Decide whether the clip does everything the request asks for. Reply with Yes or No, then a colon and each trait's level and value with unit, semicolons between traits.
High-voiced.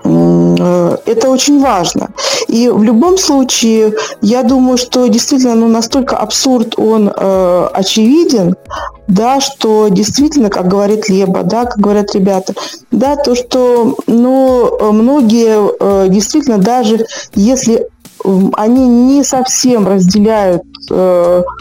Yes: high, 230 Hz